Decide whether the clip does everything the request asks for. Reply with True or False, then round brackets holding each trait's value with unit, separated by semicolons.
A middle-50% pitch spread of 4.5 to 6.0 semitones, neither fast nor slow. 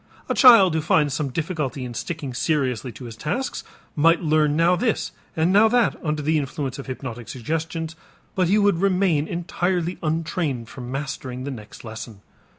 True (4.8 semitones; 170 wpm)